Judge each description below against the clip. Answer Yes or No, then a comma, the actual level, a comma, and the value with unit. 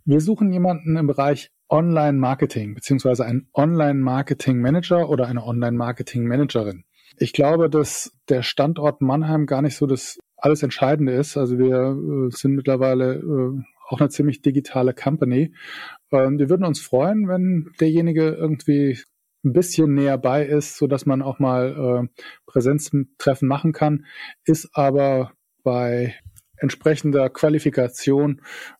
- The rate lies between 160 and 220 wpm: No, average, 135 wpm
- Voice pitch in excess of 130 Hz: Yes, medium, 140 Hz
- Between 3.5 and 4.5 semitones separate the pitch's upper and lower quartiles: No, average, 2.8 semitones